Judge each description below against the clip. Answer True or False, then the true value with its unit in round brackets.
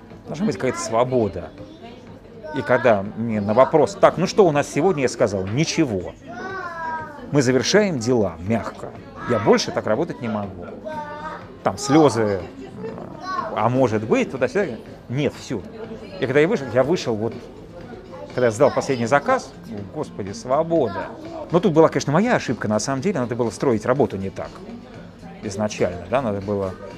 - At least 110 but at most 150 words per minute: False (160 wpm)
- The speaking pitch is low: True (130 Hz)